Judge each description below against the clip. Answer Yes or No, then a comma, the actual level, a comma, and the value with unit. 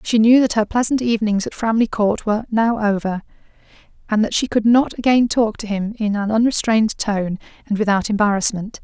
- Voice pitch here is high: Yes, high, 220 Hz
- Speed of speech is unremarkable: Yes, average, 190 wpm